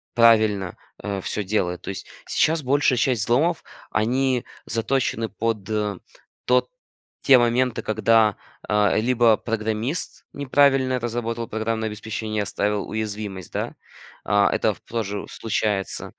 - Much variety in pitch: No, average, 3.0 semitones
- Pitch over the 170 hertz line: No, low, 110 Hz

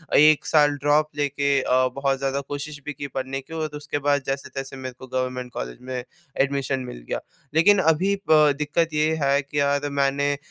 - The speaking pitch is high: No, medium, 140 Hz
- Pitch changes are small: Yes, narrow, 1.8 semitones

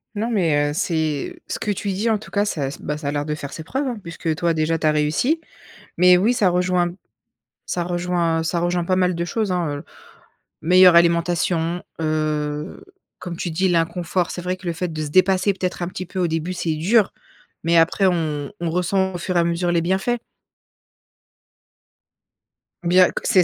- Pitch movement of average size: No, narrow, 2.3 semitones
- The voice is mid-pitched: Yes, medium, 175 Hz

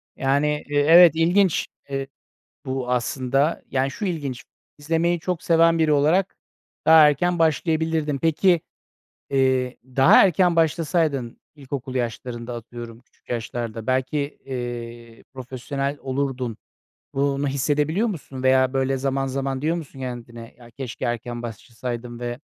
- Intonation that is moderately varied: Yes, average, 4.1 semitones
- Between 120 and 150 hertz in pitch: Yes, low, 135 Hz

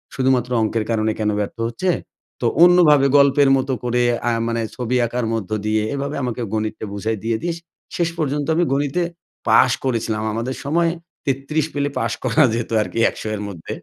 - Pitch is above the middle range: No, low, 125 Hz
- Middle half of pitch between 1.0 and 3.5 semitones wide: No, average, 4.3 semitones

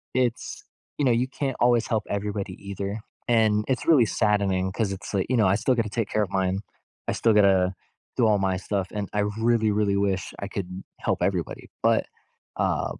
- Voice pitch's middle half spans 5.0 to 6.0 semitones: No, average, 3.0 semitones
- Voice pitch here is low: Yes, low, 105 Hz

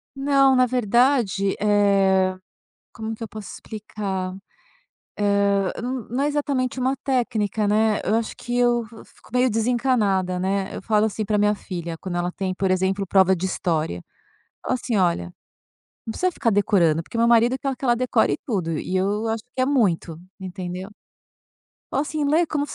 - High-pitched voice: Yes, high, 210 Hz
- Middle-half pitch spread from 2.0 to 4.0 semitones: No, average, 4.6 semitones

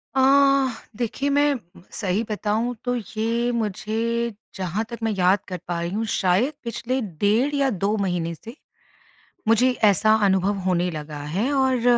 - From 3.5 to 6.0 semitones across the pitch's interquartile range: Yes, average, 4.3 semitones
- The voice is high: Yes, high, 215 Hz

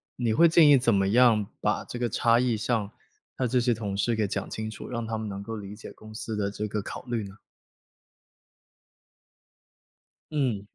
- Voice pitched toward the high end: No, low, 110 Hz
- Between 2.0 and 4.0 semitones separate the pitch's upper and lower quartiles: Yes, average, 2.7 semitones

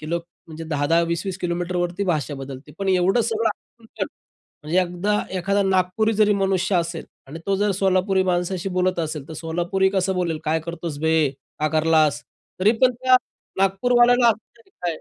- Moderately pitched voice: Yes, medium, 180 Hz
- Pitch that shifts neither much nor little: Yes, average, 3.3 semitones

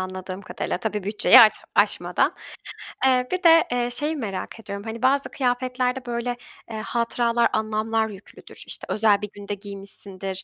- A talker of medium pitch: No, high, 225 Hz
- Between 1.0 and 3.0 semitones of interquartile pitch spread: No, average, 3.6 semitones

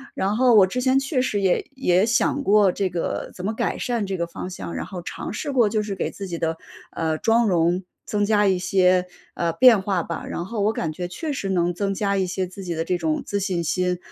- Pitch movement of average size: Yes, average, 3.2 semitones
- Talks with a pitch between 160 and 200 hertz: Yes, high, 190 Hz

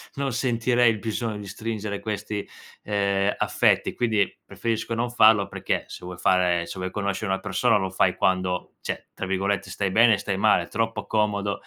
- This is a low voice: Yes, low, 105 Hz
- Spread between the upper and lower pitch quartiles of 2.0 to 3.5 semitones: Yes, average, 2.8 semitones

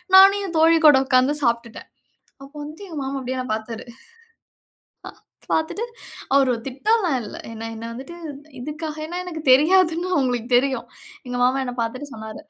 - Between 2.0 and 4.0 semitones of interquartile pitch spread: No, average, 4.7 semitones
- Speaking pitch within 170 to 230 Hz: No, very high, 275 Hz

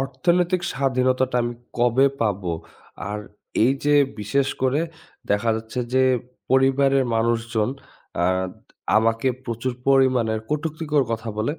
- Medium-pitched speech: No, low, 130 Hz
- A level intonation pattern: No, average, 3.3 semitones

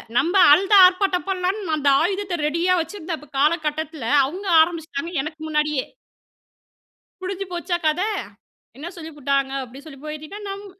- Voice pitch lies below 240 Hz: No, very high, 325 Hz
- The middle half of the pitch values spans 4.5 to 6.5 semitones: No, average, 3.5 semitones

